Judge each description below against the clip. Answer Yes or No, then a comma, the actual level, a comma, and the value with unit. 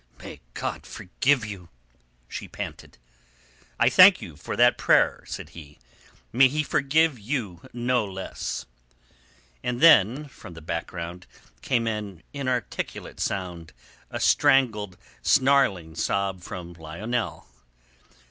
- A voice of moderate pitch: No, low, 105 Hz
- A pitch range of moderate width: No, wide, 6.7 semitones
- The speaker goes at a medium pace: No, slow, 115 wpm